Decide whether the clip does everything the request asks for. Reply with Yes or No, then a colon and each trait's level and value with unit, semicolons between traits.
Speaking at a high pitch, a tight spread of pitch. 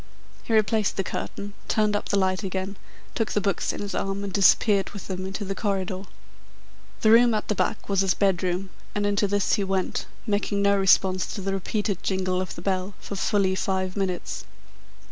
Yes: high, 195 Hz; narrow, 1.4 semitones